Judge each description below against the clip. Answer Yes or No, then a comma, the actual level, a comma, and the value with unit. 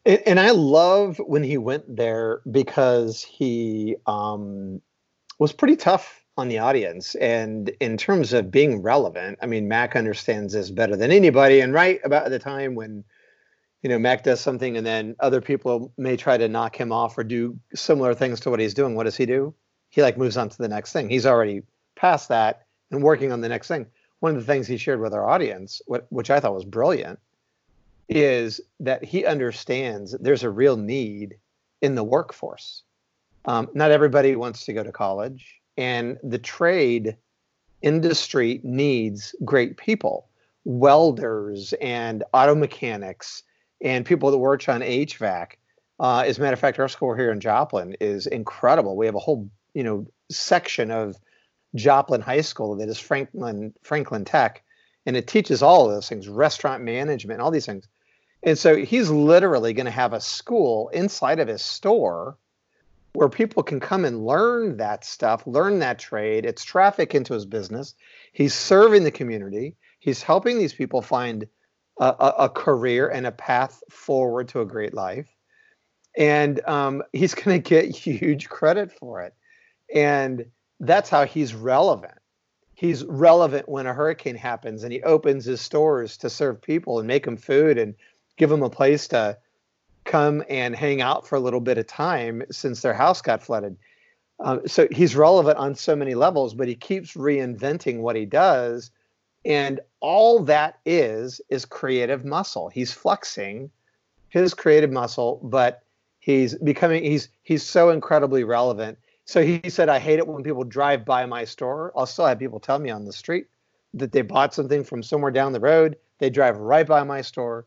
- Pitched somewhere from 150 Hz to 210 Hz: No, low, 135 Hz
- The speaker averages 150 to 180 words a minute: Yes, average, 175 wpm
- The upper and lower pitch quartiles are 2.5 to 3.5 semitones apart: No, average, 4.3 semitones